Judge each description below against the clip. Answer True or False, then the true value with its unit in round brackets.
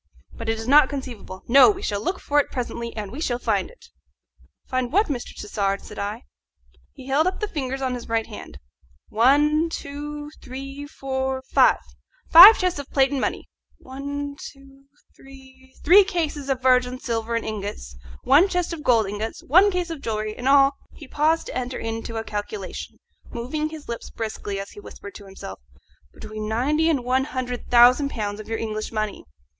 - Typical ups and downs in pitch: True (4.5 semitones)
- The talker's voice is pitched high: True (260 Hz)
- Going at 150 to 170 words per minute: False (185 wpm)